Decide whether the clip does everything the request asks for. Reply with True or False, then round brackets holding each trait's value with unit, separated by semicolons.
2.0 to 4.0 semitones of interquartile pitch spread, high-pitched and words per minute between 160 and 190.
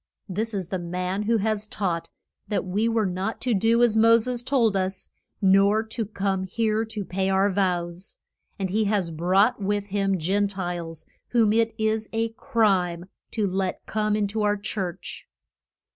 True (2.8 semitones; 200 Hz; 175 wpm)